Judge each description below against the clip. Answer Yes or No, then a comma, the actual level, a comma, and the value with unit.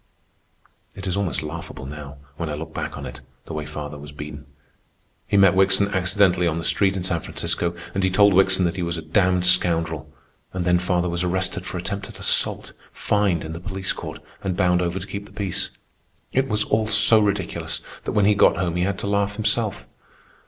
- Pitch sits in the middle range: No, very low, 90 Hz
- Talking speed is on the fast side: Yes, fast, 210 wpm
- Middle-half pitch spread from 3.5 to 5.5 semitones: No, average, 3.1 semitones